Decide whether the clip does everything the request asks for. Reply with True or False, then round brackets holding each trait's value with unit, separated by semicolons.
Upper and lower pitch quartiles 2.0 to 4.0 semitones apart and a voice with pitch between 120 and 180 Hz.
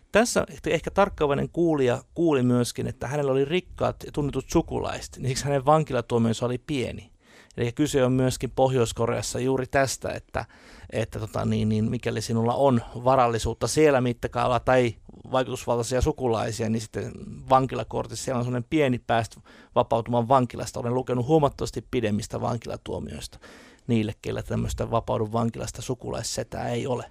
True (2.5 semitones; 125 Hz)